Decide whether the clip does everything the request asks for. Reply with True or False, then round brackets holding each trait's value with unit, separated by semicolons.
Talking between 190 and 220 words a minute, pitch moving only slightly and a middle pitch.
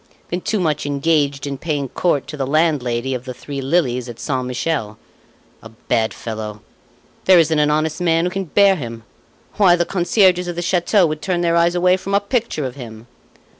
False (200 wpm; 5.4 semitones; 155 Hz)